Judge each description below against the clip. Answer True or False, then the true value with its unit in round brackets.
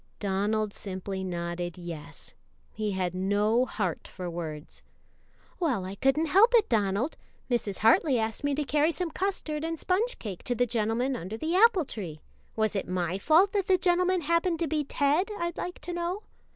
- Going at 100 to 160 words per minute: False (180 wpm)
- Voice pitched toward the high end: True (245 Hz)